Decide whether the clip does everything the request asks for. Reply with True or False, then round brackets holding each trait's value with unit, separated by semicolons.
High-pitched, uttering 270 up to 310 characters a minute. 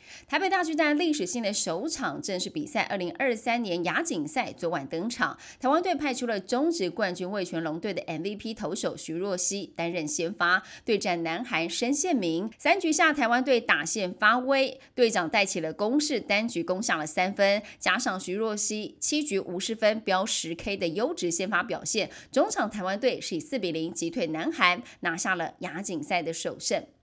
True (205 Hz; 285 characters per minute)